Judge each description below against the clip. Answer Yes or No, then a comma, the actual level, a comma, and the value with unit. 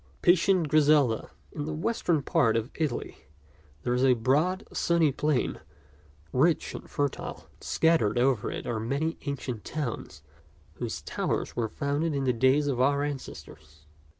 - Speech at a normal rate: Yes, average, 150 wpm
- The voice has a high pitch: No, medium, 140 Hz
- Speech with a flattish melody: No, average, 4.2 semitones